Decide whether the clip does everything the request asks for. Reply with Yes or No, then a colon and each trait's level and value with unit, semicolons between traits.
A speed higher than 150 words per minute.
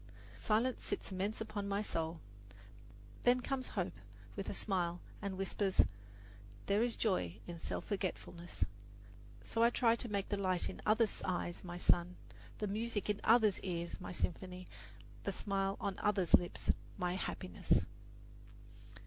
No: average, 145 wpm